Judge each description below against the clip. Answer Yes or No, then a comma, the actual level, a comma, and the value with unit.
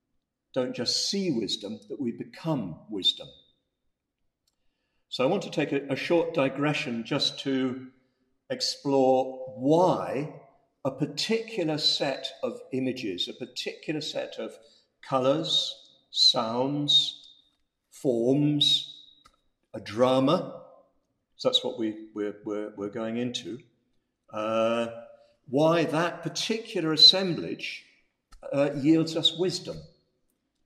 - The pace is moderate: No, slow, 105 wpm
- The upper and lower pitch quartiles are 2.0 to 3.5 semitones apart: No, average, 4.1 semitones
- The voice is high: No, medium, 140 Hz